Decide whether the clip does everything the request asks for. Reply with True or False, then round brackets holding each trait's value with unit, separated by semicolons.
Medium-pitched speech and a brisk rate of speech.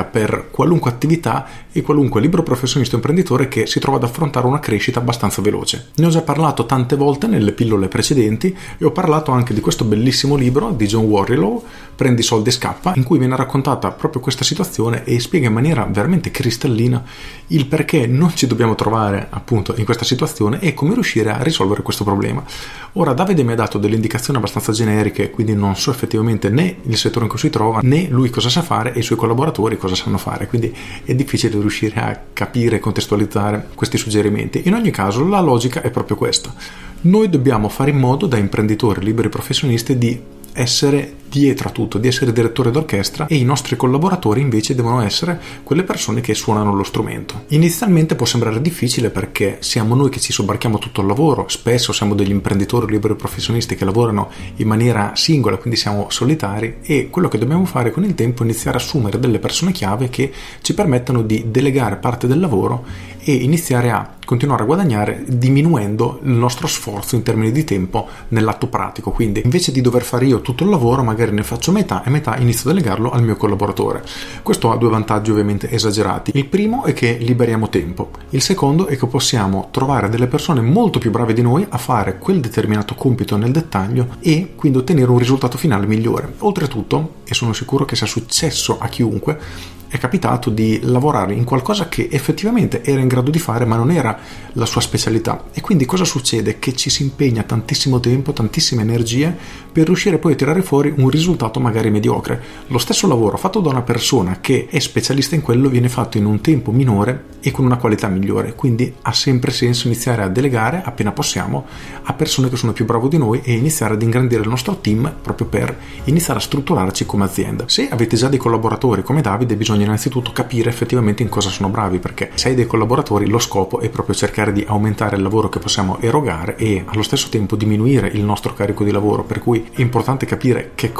False (120 Hz; 200 wpm)